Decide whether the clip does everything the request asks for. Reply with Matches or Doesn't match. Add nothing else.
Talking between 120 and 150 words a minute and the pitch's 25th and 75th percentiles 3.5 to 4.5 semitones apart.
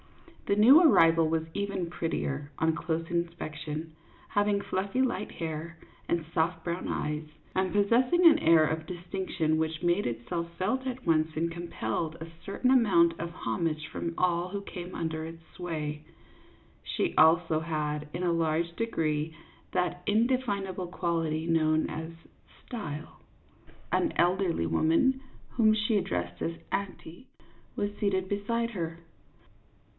Matches